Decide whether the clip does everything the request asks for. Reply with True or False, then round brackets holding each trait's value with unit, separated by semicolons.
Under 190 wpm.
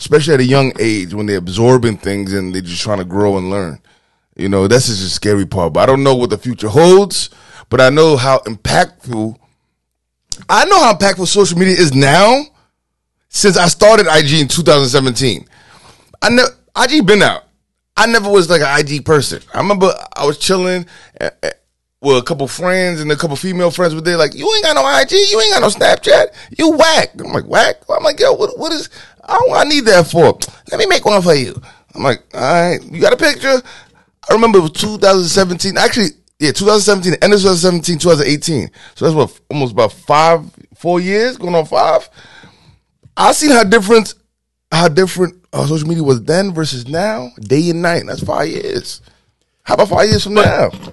False (200 wpm)